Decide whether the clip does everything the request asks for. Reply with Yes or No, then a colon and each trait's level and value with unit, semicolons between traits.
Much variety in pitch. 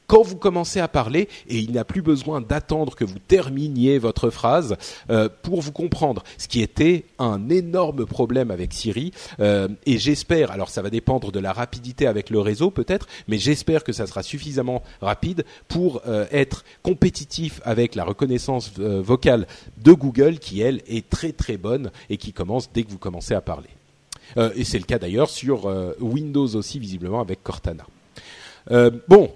Yes: wide, 5.8 semitones